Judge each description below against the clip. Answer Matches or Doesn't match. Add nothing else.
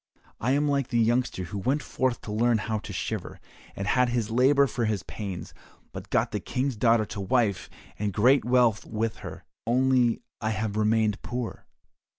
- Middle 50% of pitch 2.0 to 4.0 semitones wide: Matches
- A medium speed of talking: Matches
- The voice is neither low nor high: Doesn't match